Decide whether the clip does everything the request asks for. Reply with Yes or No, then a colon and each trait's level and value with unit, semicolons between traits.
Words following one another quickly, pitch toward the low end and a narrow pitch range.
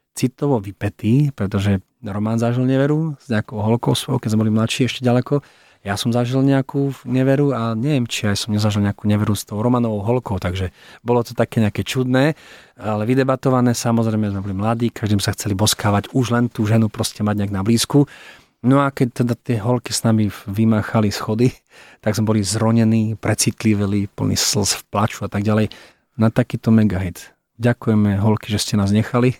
No: fast, 185 wpm; low, 110 Hz; average, 3.0 semitones